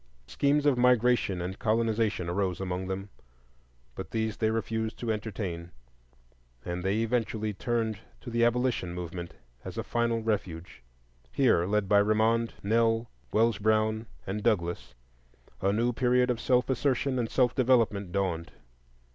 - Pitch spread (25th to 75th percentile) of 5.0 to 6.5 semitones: No, average, 3.4 semitones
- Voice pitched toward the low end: Yes, low, 110 Hz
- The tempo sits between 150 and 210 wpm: No, average, 140 wpm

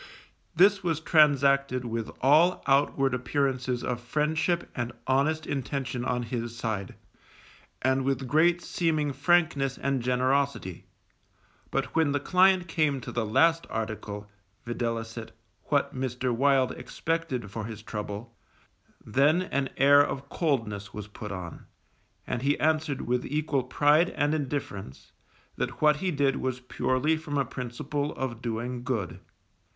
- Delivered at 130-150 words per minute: Yes, slow, 135 wpm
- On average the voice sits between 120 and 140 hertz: Yes, low, 135 Hz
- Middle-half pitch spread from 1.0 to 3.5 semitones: No, average, 3.9 semitones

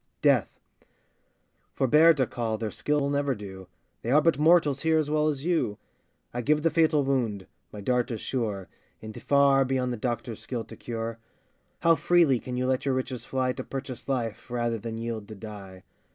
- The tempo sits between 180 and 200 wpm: Yes, average, 190 wpm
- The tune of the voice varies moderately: Yes, average, 4.1 semitones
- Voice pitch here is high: No, low, 130 Hz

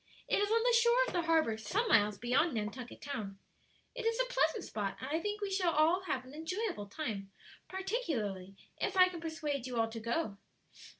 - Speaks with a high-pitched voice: Yes, very high, 315 Hz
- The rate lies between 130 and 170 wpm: No, average, 195 wpm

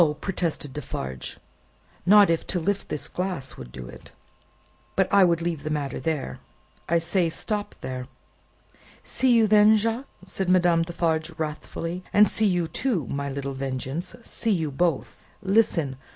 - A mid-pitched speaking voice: Yes, medium, 170 Hz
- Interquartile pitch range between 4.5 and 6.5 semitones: Yes, average, 4.9 semitones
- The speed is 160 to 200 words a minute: No, average, 150 wpm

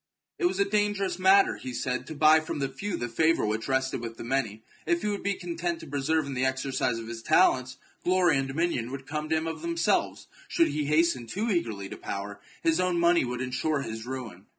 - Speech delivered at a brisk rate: Yes, fast, 225 wpm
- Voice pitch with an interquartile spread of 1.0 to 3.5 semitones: No, wide, 5.6 semitones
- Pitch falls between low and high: Yes, medium, 145 Hz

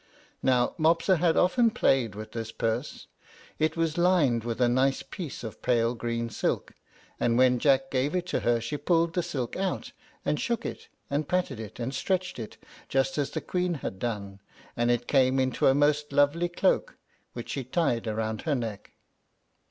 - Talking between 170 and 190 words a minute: Yes, average, 185 wpm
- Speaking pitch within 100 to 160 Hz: Yes, low, 135 Hz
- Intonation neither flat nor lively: No, wide, 5.8 semitones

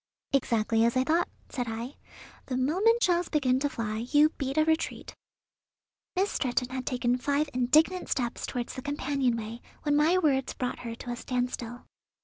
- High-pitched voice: Yes, very high, 260 Hz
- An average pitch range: Yes, average, 3.8 semitones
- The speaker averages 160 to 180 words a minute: Yes, average, 170 wpm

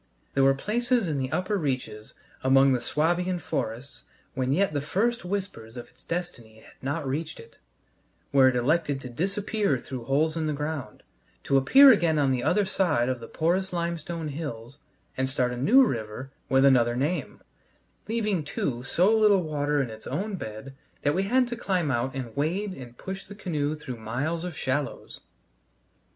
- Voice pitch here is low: No, medium, 150 Hz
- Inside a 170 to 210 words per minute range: Yes, average, 180 wpm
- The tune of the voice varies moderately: No, wide, 5.8 semitones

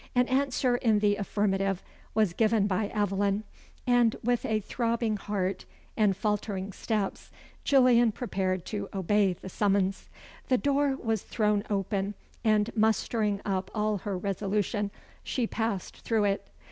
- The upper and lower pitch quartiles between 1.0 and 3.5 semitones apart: Yes, narrow, 2.4 semitones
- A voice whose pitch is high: Yes, high, 210 Hz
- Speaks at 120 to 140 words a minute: Yes, slow, 135 wpm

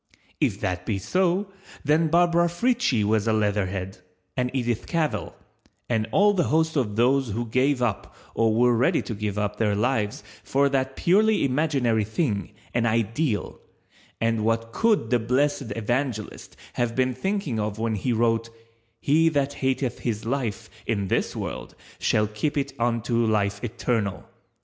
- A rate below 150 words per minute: No, average, 155 wpm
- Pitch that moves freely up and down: No, average, 4.7 semitones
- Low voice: Yes, low, 120 Hz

